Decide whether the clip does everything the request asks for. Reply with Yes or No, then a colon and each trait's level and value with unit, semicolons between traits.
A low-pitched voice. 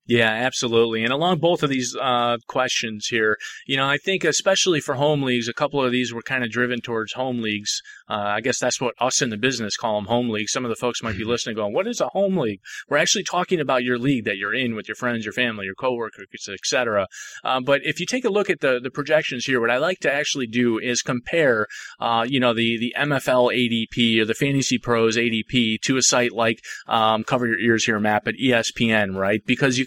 Yes: low, 125 Hz